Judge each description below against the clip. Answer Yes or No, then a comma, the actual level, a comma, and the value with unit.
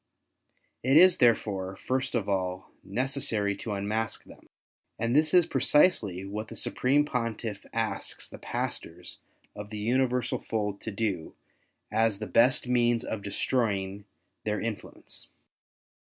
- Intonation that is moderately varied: Yes, average, 3.7 semitones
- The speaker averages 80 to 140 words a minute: Yes, slow, 135 wpm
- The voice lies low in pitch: Yes, low, 110 Hz